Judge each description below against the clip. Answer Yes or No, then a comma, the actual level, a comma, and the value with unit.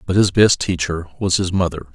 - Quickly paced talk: Yes, fast, 215 wpm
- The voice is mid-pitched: No, very low, 90 Hz